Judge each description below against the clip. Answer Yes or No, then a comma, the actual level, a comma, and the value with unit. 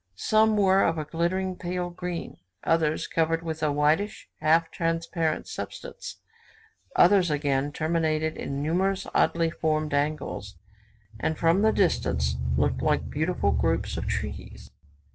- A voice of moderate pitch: Yes, medium, 165 Hz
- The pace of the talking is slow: Yes, slow, 130 wpm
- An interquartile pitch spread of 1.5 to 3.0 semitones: Yes, narrow, 2.6 semitones